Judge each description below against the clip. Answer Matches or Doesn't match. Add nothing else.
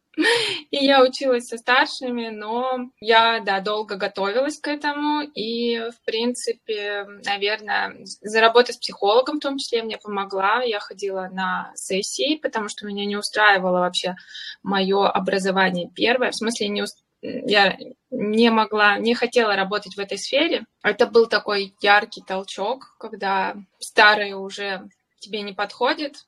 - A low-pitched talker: Doesn't match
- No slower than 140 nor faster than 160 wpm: Doesn't match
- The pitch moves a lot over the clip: Doesn't match